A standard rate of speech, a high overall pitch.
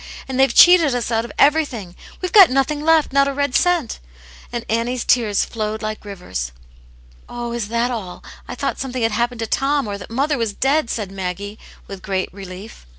No: fast, 210 wpm; high, 235 Hz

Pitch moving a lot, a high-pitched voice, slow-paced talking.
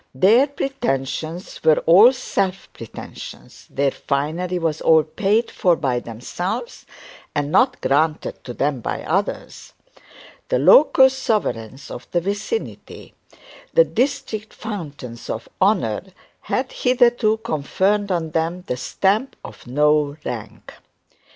No: wide, 7.4 semitones; medium, 175 Hz; slow, 120 wpm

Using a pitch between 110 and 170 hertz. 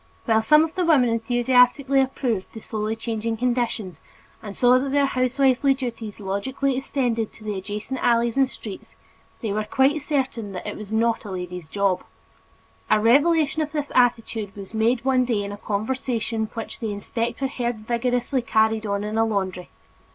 No: high, 230 Hz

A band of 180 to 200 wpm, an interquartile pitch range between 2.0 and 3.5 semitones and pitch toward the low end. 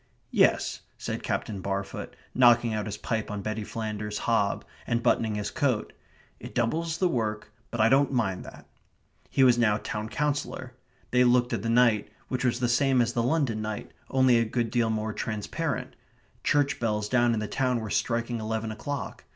Yes: average, 185 wpm; narrow, 2.6 semitones; low, 115 Hz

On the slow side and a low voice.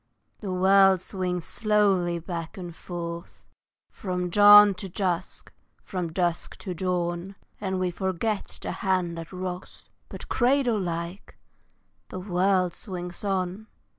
No: slow, 125 wpm; medium, 185 Hz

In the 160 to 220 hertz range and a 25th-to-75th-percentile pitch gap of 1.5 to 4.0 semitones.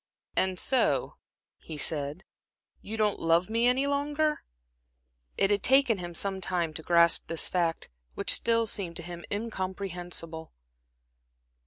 No: medium, 185 Hz; average, 5.2 semitones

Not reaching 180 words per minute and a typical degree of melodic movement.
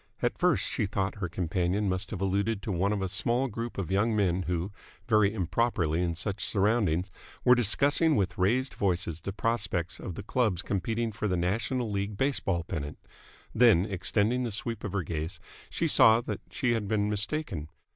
No: average, 185 wpm; average, 4.0 semitones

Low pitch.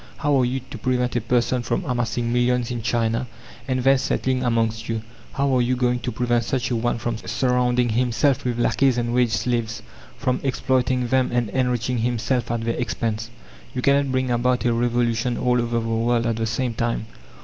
Yes: low, 120 Hz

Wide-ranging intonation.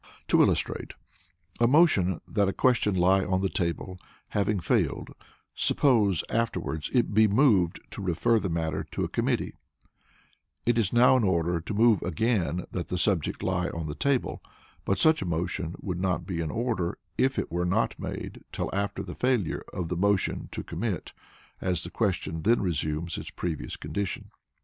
No: average, 4.5 semitones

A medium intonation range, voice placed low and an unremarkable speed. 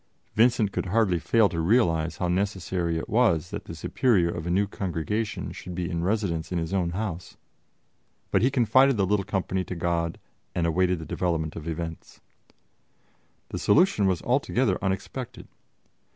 Yes: average, 3.9 semitones; very low, 90 Hz; average, 165 wpm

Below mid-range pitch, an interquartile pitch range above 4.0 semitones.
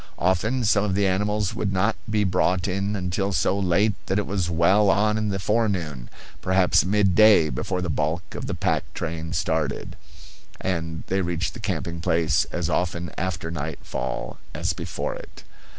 No: very low, 95 Hz; average, 3.4 semitones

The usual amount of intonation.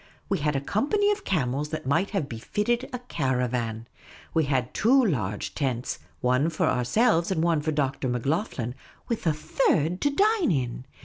No: wide, 8.5 semitones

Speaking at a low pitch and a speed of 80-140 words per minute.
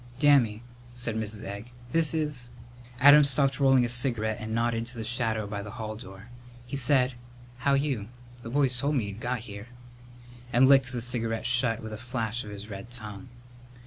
No: low, 120 Hz; average, 190 wpm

